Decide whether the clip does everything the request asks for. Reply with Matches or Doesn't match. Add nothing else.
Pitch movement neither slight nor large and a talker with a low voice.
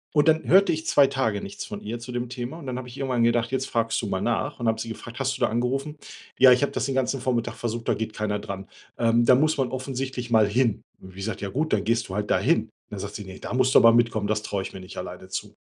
Matches